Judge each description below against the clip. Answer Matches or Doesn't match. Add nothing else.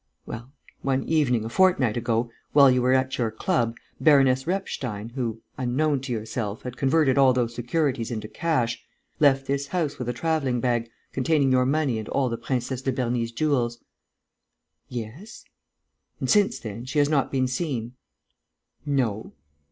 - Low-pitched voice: Matches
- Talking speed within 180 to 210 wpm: Doesn't match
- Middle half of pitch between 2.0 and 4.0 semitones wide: Matches